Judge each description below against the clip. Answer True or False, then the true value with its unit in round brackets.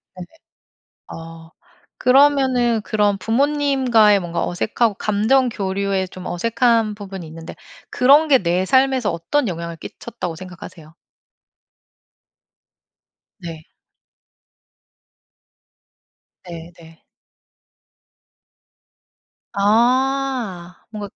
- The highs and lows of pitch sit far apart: True (6.2 semitones)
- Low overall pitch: False (205 Hz)